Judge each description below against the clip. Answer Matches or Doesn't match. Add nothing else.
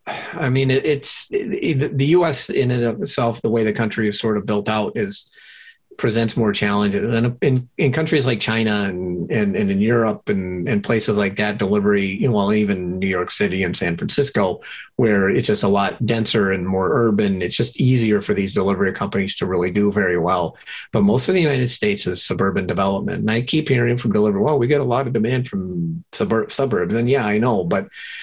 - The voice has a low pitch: Matches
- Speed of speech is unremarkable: Doesn't match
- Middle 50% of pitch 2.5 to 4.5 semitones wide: Doesn't match